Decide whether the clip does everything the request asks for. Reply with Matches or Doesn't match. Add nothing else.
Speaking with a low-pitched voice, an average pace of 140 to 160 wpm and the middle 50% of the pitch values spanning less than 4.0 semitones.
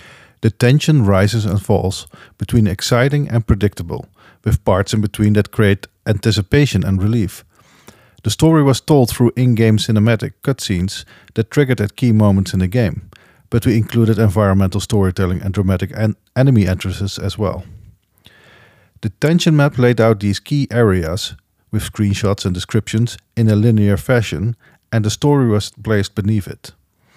Matches